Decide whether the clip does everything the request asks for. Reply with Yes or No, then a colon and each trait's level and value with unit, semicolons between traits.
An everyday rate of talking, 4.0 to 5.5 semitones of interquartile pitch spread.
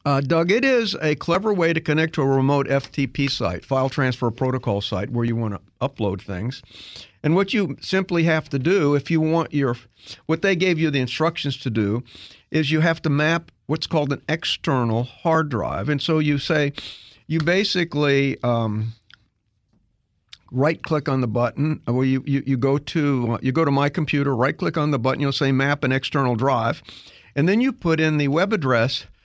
Yes: average, 195 wpm; average, 4.6 semitones